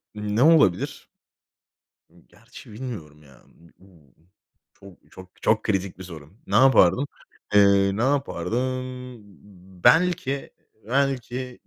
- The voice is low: Yes, low, 105 Hz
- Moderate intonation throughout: No, wide, 6.1 semitones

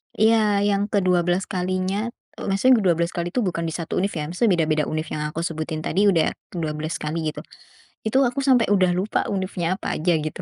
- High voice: No, medium, 180 Hz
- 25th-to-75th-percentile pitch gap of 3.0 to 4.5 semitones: Yes, average, 3.8 semitones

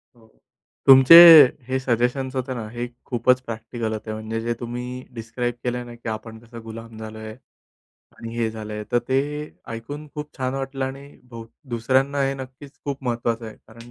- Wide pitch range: No, narrow, 2.6 semitones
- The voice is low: Yes, low, 120 Hz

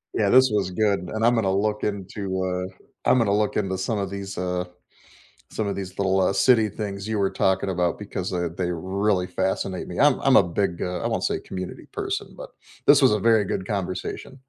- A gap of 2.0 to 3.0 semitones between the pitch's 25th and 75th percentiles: Yes, narrow, 2.6 semitones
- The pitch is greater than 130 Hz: No, low, 100 Hz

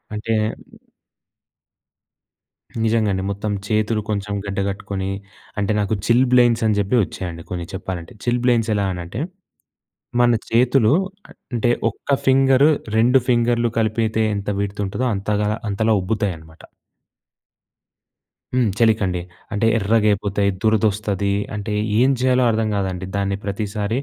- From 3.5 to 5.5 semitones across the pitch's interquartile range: No, average, 2.8 semitones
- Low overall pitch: Yes, low, 105 Hz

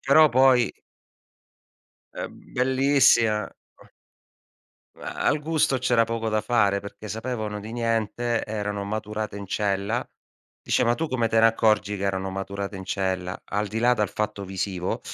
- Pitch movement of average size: Yes, average, 3.1 semitones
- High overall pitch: No, low, 110 Hz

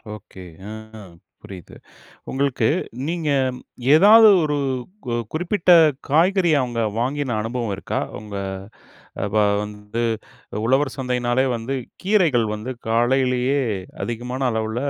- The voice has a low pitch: Yes, low, 125 Hz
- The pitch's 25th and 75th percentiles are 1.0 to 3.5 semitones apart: No, average, 4.6 semitones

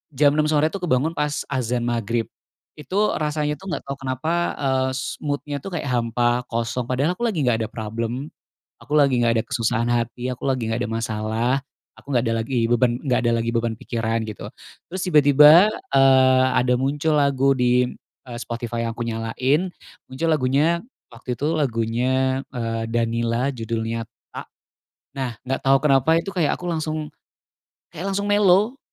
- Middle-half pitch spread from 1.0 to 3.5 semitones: No, average, 4.1 semitones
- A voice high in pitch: No, low, 130 Hz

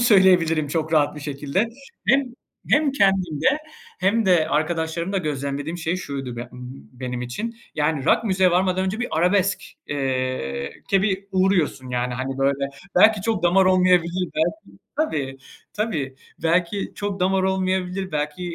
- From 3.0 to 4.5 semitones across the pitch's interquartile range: No, average, 5.2 semitones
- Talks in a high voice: No, medium, 175 Hz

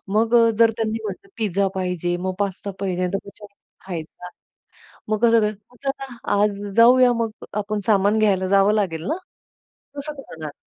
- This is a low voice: No, high, 205 Hz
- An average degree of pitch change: Yes, average, 3.1 semitones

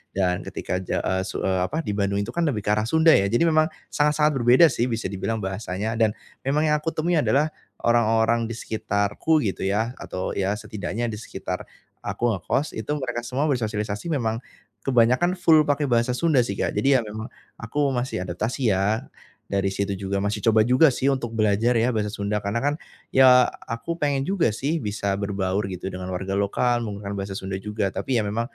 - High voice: No, low, 115 Hz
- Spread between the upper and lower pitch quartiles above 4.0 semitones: Yes, average, 4.7 semitones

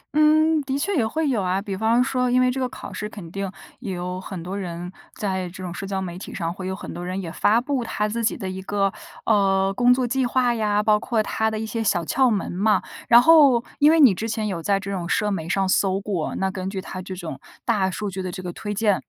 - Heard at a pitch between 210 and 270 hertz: No, high, 200 Hz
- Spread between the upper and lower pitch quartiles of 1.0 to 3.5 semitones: No, average, 4.1 semitones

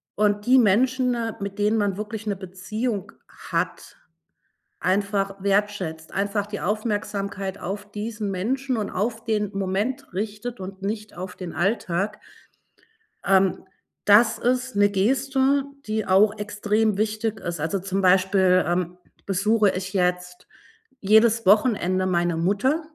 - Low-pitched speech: No, high, 205 Hz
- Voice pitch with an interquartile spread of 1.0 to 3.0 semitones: Yes, narrow, 2.5 semitones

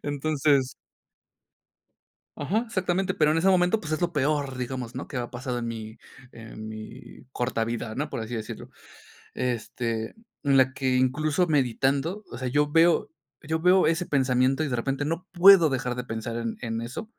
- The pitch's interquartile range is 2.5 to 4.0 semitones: No, average, 4.6 semitones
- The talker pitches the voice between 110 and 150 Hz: Yes, low, 135 Hz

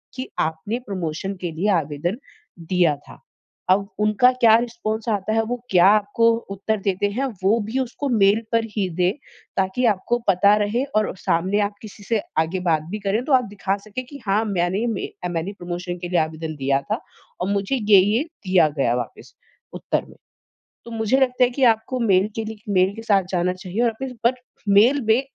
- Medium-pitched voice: No, high, 205 Hz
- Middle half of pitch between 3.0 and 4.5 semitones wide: Yes, average, 3.7 semitones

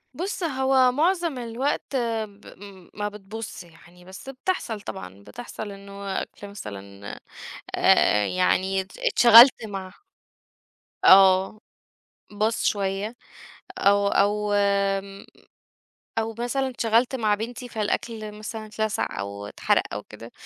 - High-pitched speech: Yes, high, 210 Hz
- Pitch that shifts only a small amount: No, average, 3.4 semitones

